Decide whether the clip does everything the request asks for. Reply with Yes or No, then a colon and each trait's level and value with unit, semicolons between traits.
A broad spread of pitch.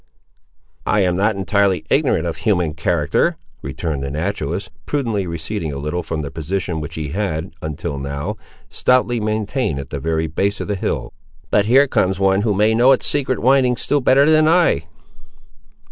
Yes: wide, 5.9 semitones